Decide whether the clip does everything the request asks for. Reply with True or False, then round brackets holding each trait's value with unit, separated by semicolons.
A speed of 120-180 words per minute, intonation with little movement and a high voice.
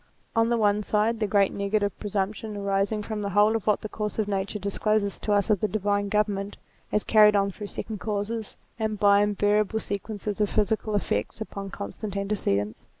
False (190 wpm; 1.2 semitones; 205 Hz)